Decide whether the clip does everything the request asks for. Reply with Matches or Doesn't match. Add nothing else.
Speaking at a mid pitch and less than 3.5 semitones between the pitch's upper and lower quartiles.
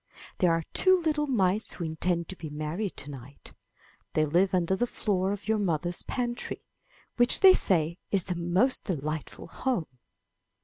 Doesn't match